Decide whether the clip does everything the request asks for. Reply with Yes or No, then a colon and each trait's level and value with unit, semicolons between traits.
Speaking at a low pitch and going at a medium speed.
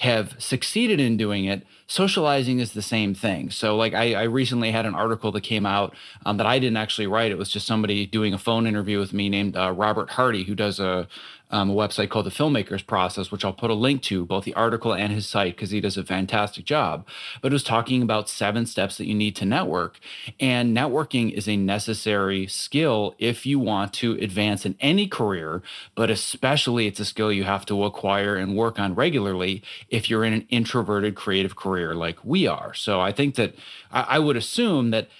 No: low, 105 Hz; fast, 215 wpm